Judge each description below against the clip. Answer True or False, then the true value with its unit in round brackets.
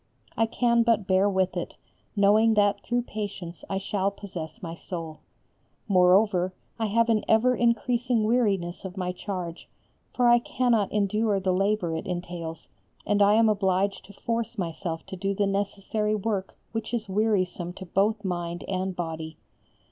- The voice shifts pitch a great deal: False (3.3 semitones)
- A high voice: True (200 Hz)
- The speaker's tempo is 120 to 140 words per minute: False (160 wpm)